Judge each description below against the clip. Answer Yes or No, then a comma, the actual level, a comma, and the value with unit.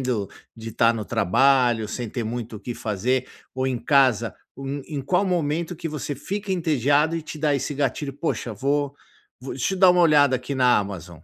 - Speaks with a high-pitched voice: No, low, 135 Hz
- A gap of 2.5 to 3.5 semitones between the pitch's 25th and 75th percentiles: No, average, 4.2 semitones